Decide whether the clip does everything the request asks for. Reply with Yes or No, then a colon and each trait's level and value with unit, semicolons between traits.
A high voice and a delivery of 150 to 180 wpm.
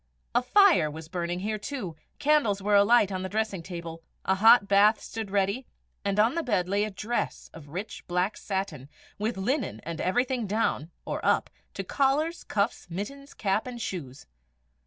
Yes: high, 205 Hz; average, 170 wpm